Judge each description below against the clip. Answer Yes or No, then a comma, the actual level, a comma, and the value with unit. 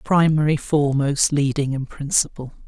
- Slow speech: Yes, slow, 110 wpm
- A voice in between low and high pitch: Yes, medium, 145 Hz